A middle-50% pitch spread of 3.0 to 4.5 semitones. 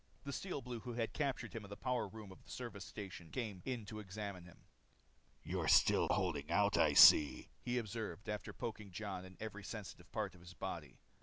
Yes: average, 3.7 semitones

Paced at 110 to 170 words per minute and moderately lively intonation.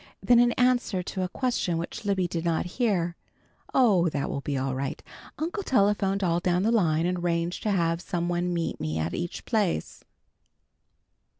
No: average, 180 wpm; average, 3.7 semitones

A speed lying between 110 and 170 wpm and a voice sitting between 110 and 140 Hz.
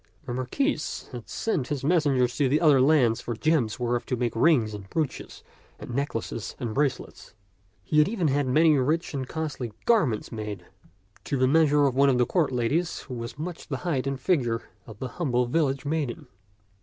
No: average, 190 wpm; low, 135 Hz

